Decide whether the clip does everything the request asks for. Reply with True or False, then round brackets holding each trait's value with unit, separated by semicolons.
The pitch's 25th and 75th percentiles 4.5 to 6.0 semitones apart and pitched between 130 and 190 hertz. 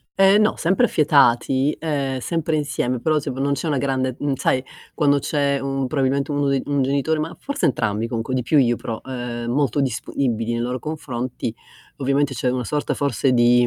False (2.8 semitones; 135 Hz)